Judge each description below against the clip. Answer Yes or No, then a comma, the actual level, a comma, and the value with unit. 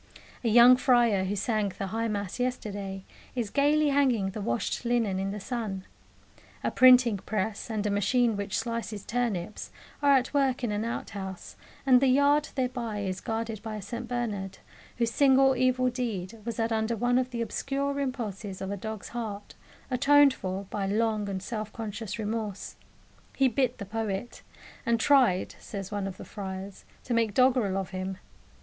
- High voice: Yes, high, 225 Hz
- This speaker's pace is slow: No, average, 175 wpm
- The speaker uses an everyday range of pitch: Yes, average, 3.8 semitones